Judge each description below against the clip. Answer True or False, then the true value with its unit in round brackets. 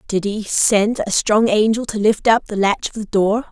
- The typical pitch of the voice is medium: False (210 Hz)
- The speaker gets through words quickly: True (240 wpm)